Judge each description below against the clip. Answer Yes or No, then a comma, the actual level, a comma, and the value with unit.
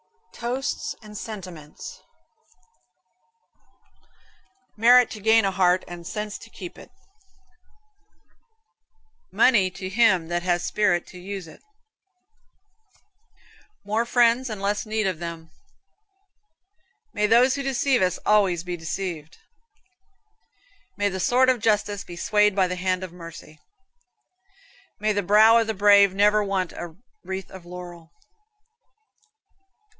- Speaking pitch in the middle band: No, high, 195 Hz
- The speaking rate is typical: No, slow, 120 wpm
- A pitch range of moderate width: Yes, average, 3.2 semitones